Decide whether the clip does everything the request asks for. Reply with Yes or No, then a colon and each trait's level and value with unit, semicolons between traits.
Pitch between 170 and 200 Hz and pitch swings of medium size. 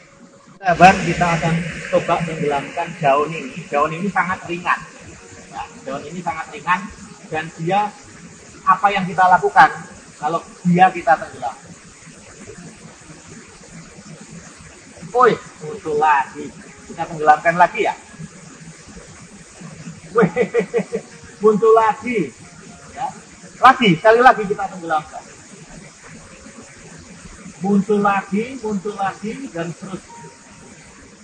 Yes: medium, 185 Hz; average, 4.0 semitones